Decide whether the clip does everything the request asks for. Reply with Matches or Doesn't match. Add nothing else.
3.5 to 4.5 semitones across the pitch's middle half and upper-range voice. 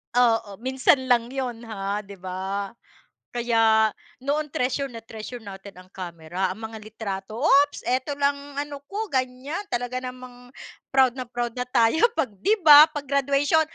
Matches